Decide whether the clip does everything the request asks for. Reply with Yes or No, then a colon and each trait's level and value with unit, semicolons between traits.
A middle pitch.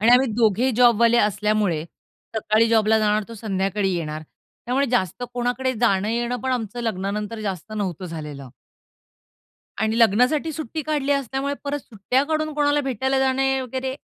No: high, 230 Hz